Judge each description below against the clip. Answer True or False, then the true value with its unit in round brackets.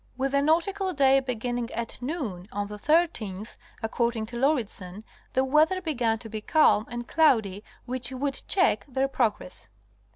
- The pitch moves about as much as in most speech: True (4.7 semitones)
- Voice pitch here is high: True (250 Hz)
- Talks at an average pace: True (155 wpm)